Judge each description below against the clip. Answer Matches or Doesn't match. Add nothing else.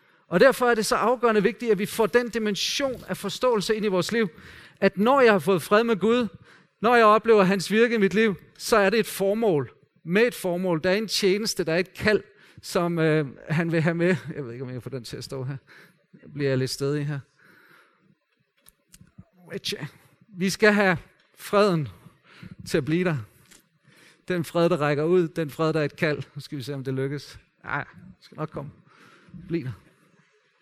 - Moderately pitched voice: Matches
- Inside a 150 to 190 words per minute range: Doesn't match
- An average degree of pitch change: Doesn't match